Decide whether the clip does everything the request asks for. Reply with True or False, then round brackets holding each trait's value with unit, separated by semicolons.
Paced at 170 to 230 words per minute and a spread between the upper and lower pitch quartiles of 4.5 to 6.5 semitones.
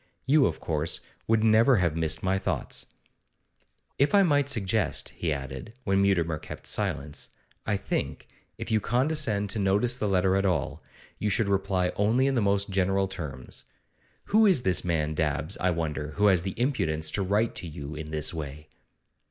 True (175 wpm; 5.6 semitones)